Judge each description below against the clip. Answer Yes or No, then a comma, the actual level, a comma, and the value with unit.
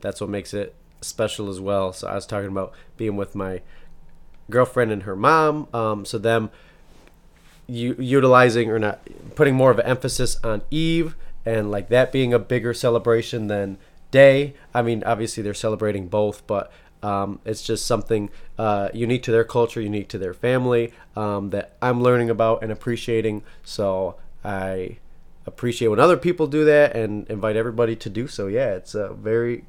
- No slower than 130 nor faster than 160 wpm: No, average, 175 wpm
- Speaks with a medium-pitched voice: No, low, 115 Hz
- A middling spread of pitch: Yes, average, 3.2 semitones